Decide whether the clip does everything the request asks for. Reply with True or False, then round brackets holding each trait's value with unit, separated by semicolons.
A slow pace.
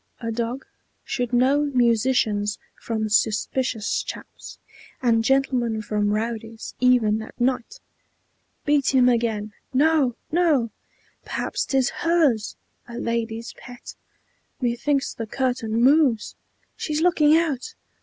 True (115 wpm)